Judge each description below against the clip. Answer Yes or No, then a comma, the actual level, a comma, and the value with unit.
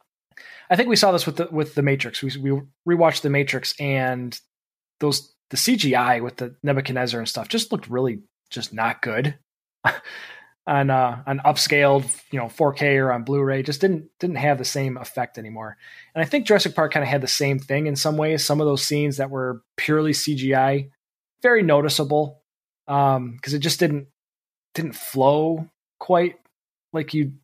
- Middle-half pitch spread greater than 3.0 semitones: No, narrow, 2.6 semitones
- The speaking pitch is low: No, medium, 145 Hz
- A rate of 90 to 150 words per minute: No, average, 185 wpm